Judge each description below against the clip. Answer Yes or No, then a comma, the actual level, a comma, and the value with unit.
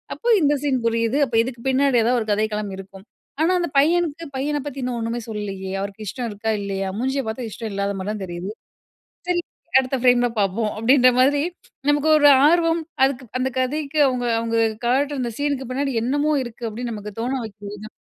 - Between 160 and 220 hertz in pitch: No, high, 245 Hz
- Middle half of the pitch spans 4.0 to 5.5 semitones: Yes, average, 4.7 semitones